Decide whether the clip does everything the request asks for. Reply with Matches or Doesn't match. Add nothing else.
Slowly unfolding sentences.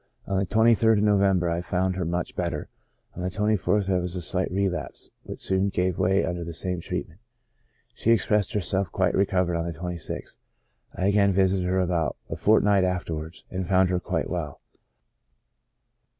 Doesn't match